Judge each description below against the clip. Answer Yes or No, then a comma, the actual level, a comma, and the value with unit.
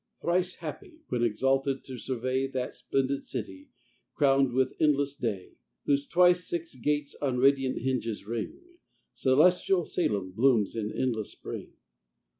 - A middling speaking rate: No, slow, 130 wpm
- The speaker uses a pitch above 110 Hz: Yes, low, 135 Hz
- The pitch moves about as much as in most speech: Yes, average, 3.4 semitones